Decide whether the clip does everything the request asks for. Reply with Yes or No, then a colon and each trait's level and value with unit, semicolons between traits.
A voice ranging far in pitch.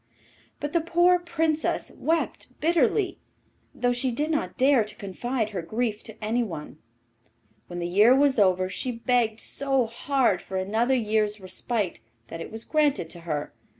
Yes: wide, 5.7 semitones